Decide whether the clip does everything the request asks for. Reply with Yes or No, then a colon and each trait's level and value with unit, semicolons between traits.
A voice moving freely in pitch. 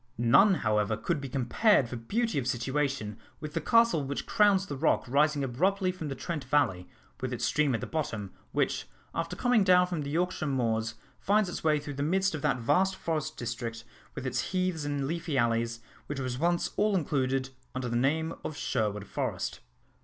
Yes: wide, 6.0 semitones